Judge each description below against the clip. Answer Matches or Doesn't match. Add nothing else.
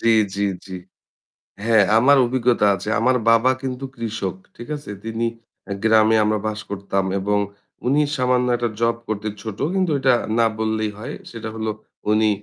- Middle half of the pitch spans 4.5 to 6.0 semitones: Doesn't match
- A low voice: Matches